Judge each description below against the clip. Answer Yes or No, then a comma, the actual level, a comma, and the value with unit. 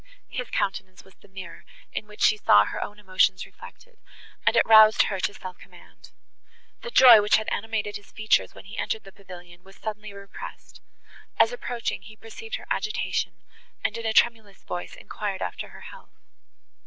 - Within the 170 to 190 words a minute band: Yes, average, 180 wpm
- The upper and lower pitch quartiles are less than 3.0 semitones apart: Yes, narrow, 2.6 semitones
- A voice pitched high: Yes, high, 210 Hz